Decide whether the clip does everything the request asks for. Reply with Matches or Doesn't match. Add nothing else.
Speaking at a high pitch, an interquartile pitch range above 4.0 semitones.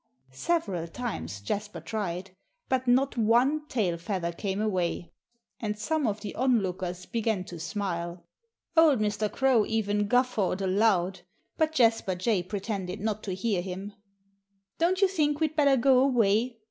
Matches